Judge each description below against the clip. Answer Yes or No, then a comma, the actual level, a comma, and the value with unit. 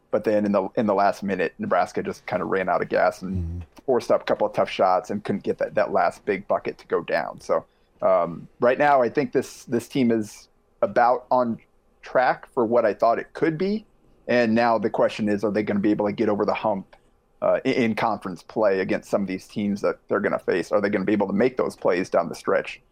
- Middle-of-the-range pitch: No, low, 105 Hz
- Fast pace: Yes, fast, 260 wpm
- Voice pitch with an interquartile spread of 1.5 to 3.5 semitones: Yes, average, 2.7 semitones